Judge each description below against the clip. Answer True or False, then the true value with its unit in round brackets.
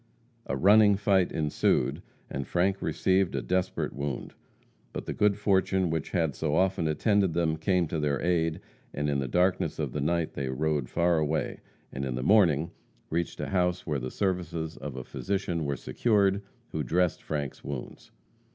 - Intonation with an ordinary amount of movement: True (4.3 semitones)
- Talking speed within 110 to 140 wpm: False (175 wpm)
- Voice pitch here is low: True (85 Hz)